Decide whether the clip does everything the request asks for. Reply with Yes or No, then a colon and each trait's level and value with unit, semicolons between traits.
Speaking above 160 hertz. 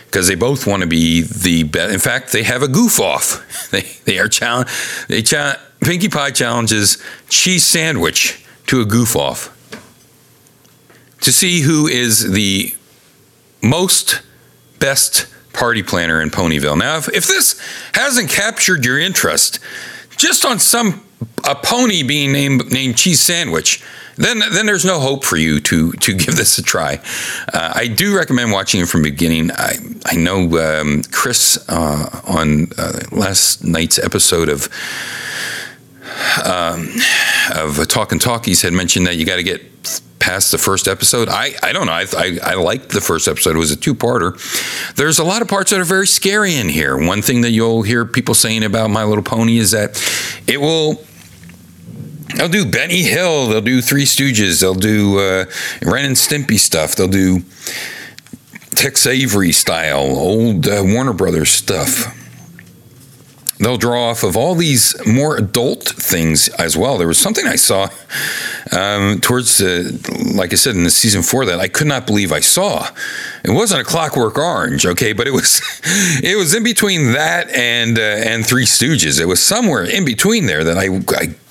No: low, 115 Hz